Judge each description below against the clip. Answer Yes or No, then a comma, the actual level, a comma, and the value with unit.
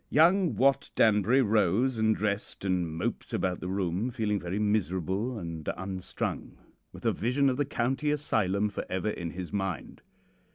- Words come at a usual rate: Yes, average, 160 wpm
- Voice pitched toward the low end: Yes, low, 105 Hz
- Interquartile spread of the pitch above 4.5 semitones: Yes, average, 4.9 semitones